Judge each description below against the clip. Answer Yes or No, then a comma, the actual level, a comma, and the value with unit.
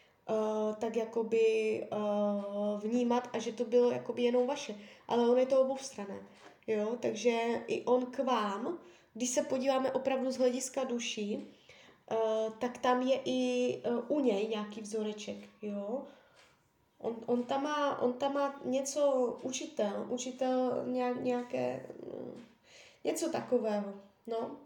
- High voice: Yes, high, 245 Hz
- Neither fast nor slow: Yes, average, 140 wpm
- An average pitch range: Yes, average, 3.2 semitones